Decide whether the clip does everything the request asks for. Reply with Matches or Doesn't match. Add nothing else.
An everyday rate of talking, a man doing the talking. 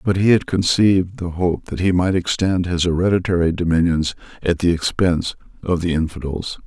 Matches